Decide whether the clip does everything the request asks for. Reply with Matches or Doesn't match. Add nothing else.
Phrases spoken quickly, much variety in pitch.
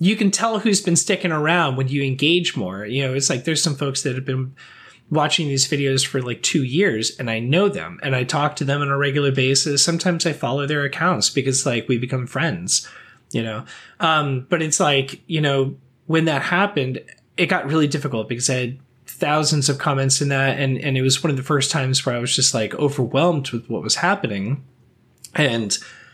Doesn't match